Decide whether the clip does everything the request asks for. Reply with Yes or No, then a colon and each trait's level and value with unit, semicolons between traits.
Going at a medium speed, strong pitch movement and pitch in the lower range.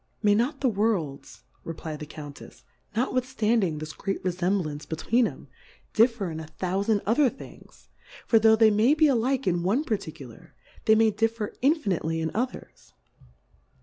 No: average, 155 wpm; wide, 6.1 semitones; high, 210 Hz